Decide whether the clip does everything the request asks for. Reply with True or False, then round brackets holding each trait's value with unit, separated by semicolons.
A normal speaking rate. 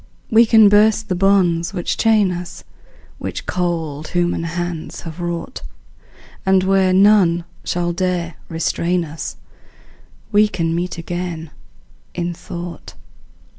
False (120 wpm)